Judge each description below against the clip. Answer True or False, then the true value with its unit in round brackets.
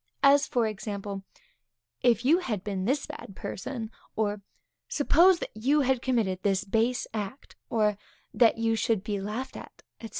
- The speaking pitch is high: True (225 Hz)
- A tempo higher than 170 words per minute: False (160 wpm)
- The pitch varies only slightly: False (4.1 semitones)